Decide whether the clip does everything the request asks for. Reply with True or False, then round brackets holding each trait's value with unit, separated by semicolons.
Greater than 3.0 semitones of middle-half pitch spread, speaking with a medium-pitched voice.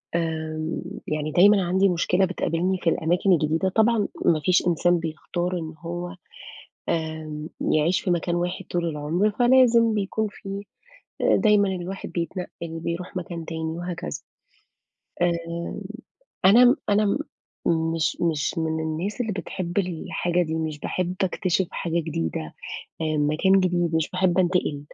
False (2.7 semitones; 175 Hz)